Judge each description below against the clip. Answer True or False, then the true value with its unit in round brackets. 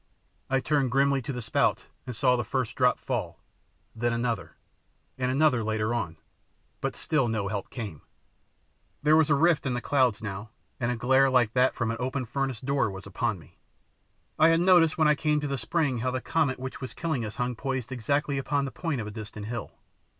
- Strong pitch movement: False (3.5 semitones)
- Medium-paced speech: False (210 wpm)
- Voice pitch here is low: True (130 Hz)